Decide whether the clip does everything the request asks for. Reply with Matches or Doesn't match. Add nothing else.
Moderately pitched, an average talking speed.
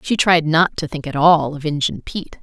Doesn't match